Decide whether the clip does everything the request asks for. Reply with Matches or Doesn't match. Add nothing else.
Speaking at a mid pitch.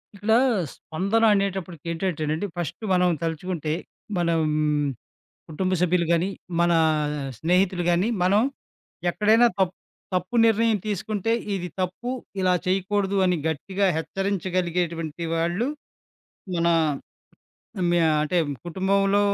Matches